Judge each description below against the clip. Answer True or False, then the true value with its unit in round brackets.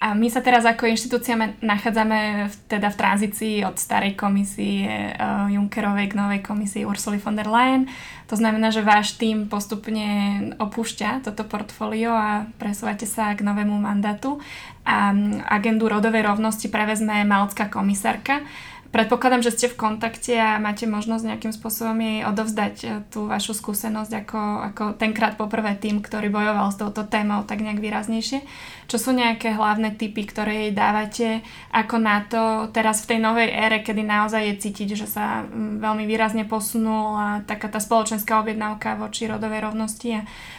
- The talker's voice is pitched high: True (215 Hz)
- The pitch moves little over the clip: True (1.2 semitones)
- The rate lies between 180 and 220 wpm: False (155 wpm)